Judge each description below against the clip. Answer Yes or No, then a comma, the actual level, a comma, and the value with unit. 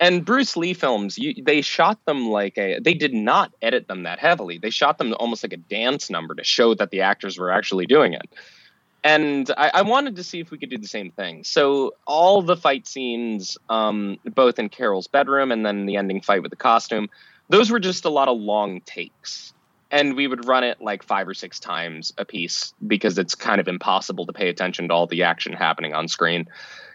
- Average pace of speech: No, fast, 225 wpm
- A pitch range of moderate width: No, wide, 8.1 semitones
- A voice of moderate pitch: No, low, 130 Hz